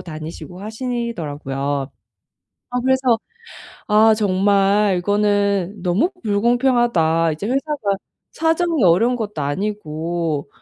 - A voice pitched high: Yes, high, 205 Hz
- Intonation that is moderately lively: No, wide, 6.1 semitones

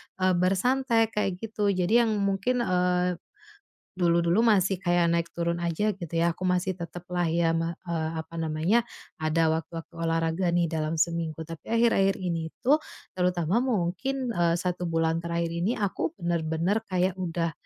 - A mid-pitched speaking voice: Yes, medium, 175 Hz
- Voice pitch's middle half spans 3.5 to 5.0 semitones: No, average, 2.8 semitones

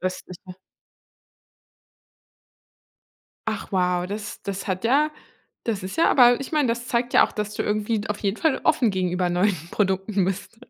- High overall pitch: Yes, high, 205 Hz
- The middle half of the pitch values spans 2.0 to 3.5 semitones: No, average, 4.0 semitones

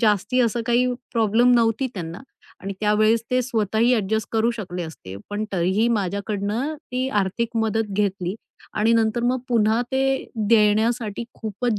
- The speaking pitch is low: No, high, 220 Hz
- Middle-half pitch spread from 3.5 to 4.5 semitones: No, average, 2.7 semitones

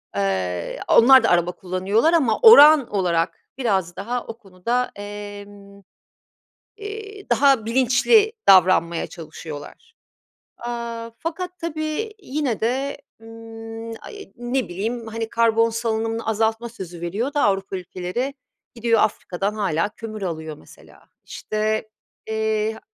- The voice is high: Yes, high, 225 Hz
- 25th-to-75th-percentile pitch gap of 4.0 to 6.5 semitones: Yes, average, 4.4 semitones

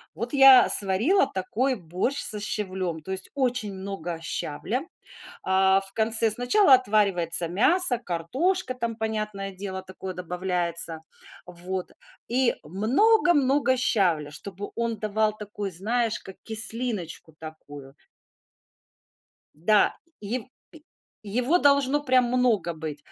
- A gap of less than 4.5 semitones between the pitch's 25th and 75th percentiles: No, average, 5.3 semitones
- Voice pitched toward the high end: Yes, high, 210 Hz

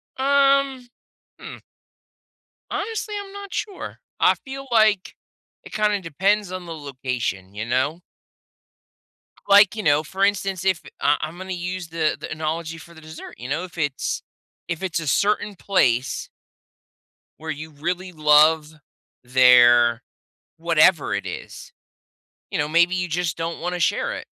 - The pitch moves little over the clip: No, average, 4.7 semitones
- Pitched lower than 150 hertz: No, medium, 170 Hz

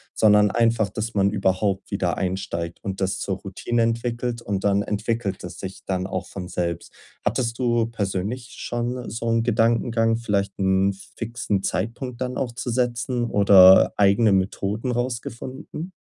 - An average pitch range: Yes, average, 3.4 semitones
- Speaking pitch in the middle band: No, low, 110 Hz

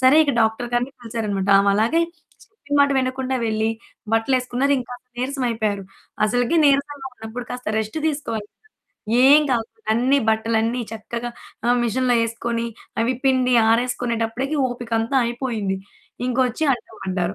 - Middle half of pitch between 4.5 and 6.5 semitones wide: No, narrow, 2.6 semitones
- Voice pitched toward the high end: Yes, high, 240 Hz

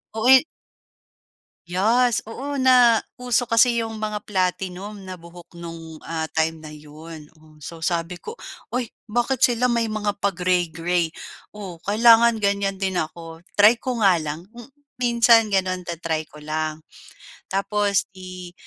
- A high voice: Yes, high, 195 Hz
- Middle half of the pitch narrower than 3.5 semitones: No, average, 5.3 semitones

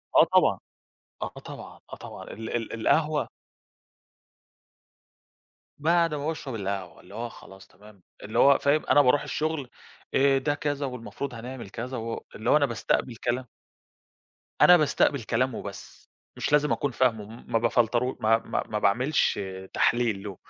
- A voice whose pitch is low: Yes, low, 125 Hz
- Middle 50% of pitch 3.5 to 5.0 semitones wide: Yes, average, 4.3 semitones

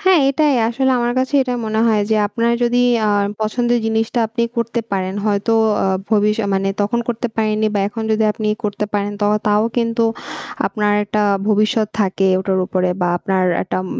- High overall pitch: Yes, high, 220 Hz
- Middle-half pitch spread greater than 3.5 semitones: No, narrow, 2.5 semitones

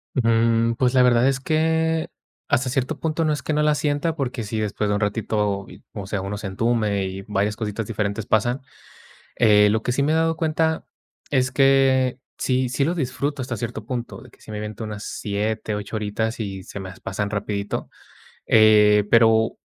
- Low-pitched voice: Yes, low, 115 Hz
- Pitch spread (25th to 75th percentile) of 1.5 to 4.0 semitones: No, average, 4.5 semitones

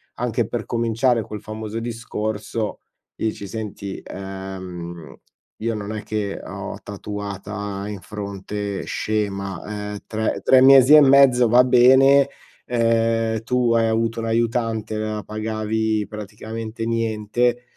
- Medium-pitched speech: No, low, 110 Hz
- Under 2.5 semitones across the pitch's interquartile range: Yes, narrow, 2.0 semitones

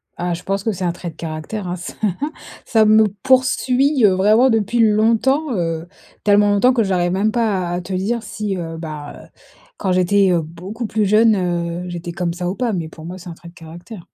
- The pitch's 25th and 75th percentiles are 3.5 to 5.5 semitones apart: Yes, average, 4.0 semitones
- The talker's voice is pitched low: No, high, 190 Hz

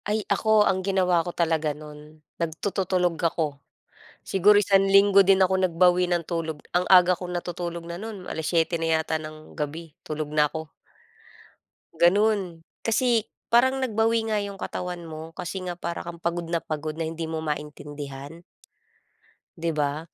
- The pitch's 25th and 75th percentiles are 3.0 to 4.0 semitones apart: Yes, average, 3.3 semitones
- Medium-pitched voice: Yes, medium, 170 Hz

